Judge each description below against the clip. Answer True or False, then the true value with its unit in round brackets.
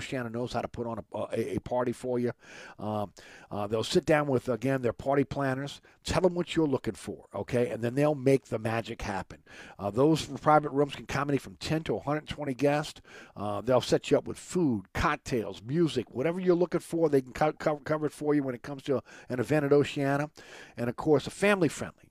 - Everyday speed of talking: False (225 wpm)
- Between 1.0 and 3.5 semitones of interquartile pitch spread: False (4.1 semitones)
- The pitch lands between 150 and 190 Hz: False (135 Hz)